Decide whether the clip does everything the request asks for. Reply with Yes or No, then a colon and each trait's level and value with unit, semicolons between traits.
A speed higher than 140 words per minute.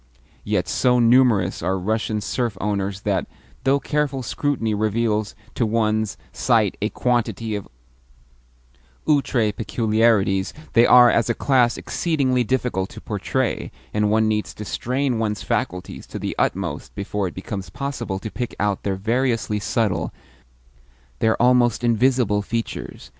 No: slow, 135 wpm